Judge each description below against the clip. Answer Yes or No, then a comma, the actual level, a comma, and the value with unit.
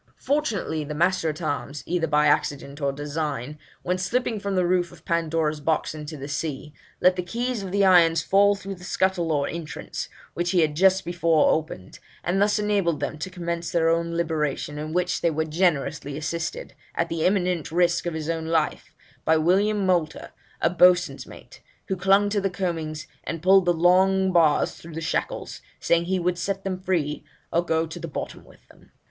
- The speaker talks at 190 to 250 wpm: Yes, average, 195 wpm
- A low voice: No, medium, 170 Hz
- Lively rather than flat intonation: No, average, 3.1 semitones